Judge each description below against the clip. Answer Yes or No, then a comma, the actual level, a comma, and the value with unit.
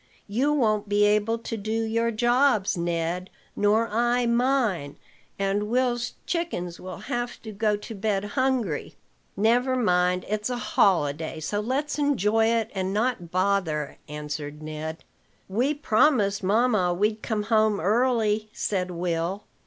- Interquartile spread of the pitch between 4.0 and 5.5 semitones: Yes, average, 4.5 semitones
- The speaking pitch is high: Yes, high, 210 Hz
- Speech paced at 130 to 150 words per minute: Yes, slow, 135 wpm